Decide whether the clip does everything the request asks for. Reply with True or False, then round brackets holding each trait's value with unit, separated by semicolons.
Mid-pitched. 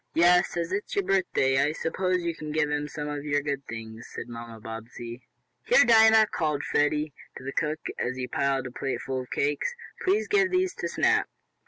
True (150 Hz)